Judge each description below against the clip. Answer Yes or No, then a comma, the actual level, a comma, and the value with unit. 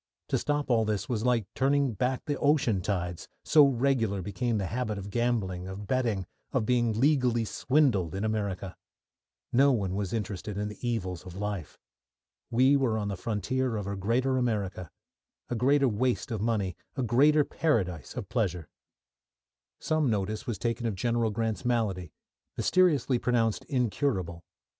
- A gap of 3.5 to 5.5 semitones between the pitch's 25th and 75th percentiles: Yes, average, 4.3 semitones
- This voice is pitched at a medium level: No, low, 115 Hz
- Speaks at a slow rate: No, average, 155 wpm